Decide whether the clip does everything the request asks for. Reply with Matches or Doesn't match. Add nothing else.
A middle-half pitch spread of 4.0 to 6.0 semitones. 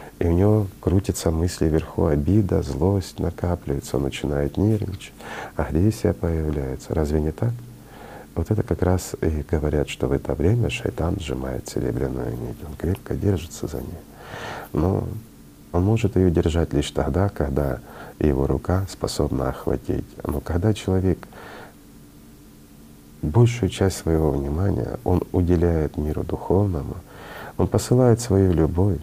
Matches